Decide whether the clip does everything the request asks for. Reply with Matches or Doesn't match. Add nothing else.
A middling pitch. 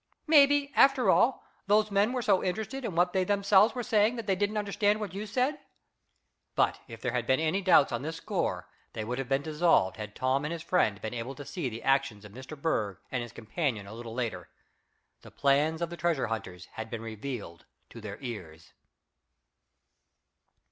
Matches